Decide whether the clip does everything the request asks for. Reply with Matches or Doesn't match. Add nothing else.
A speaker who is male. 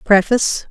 Doesn't match